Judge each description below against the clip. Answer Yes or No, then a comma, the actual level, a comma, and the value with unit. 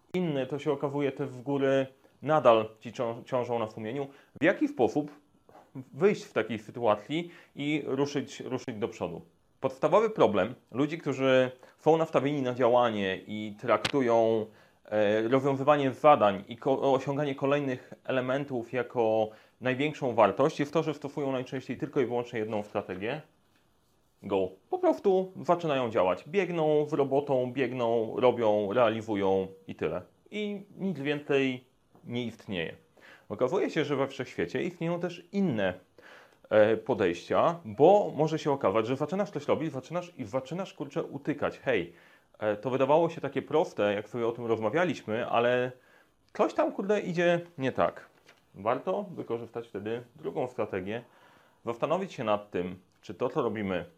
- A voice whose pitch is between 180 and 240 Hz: No, low, 135 Hz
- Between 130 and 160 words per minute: Yes, average, 140 wpm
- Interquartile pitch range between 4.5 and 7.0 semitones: Yes, average, 4.9 semitones